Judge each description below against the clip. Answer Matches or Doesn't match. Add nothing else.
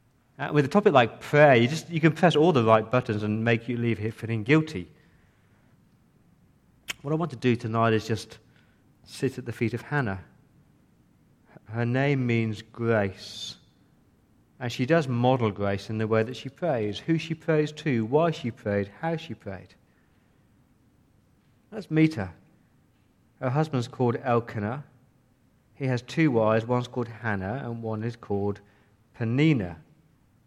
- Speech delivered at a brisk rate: Doesn't match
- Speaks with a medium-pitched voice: Doesn't match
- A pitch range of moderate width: Matches